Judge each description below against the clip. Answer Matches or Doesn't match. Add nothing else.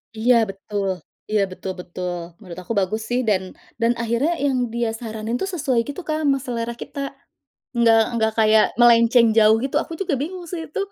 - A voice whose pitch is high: Matches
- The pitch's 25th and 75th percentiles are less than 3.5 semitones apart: Doesn't match